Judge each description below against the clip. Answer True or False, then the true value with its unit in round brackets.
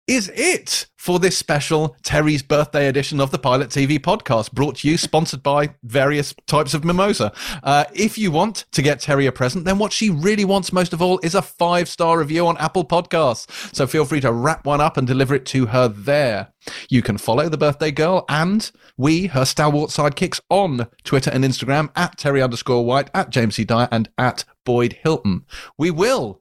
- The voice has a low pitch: False (150 Hz)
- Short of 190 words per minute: False (200 wpm)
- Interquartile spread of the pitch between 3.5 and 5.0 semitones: True (4.2 semitones)